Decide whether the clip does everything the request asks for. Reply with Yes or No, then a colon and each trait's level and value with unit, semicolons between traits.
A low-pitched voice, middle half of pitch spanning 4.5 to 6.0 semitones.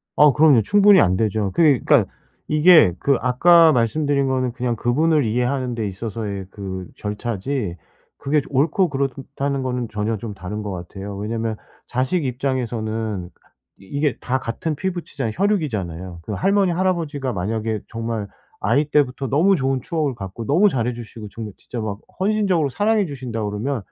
Yes: low, 125 Hz; wide, 5.6 semitones